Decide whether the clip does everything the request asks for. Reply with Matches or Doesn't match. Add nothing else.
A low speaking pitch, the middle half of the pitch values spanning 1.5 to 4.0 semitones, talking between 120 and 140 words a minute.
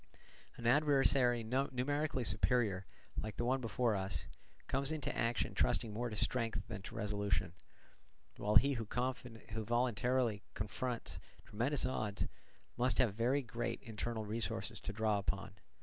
Matches